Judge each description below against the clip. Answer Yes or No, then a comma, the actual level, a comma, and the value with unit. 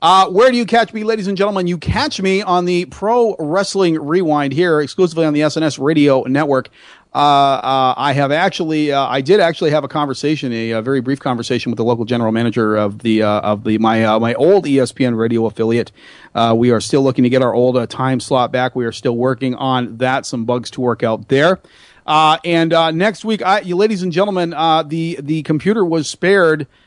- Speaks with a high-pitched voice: No, medium, 140 Hz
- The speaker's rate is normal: No, fast, 220 wpm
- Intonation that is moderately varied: No, wide, 6.2 semitones